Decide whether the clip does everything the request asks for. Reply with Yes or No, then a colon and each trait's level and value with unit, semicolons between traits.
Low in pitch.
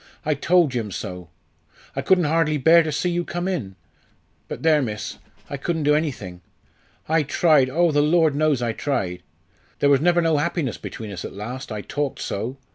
No: medium, 145 Hz